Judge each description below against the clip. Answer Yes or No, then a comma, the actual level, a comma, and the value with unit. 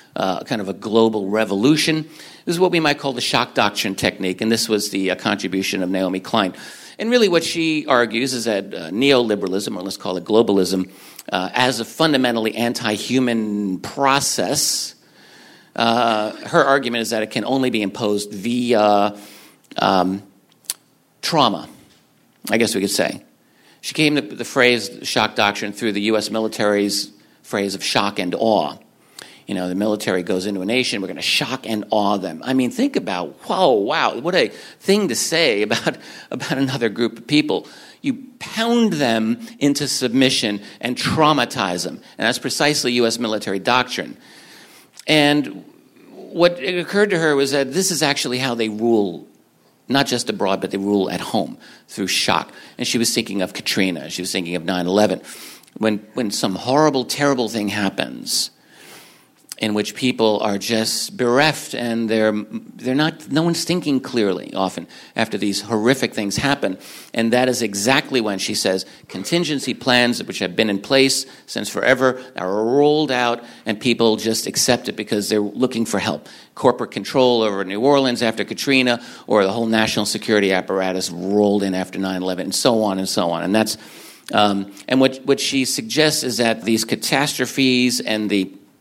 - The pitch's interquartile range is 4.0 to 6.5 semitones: Yes, average, 4.7 semitones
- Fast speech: No, average, 175 wpm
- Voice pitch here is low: Yes, low, 115 Hz